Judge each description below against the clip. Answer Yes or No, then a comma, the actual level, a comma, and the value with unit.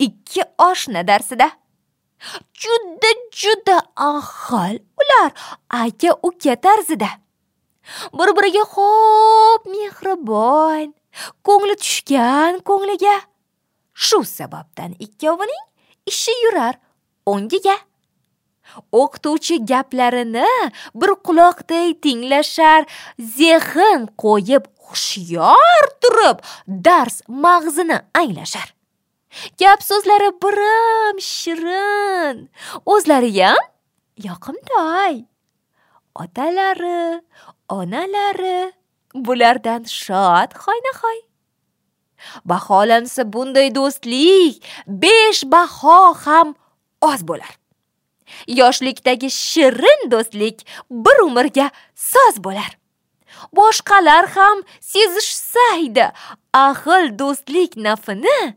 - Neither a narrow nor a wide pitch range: No, wide, 7.8 semitones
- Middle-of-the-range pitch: No, very high, 335 Hz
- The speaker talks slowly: Yes, slow, 70 wpm